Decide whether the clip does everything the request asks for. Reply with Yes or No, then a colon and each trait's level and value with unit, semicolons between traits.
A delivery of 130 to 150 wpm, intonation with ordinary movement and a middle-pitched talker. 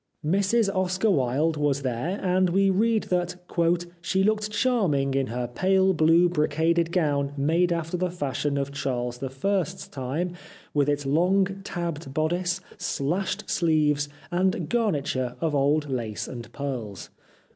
Yes: average, 140 wpm; average, 4.8 semitones; medium, 160 Hz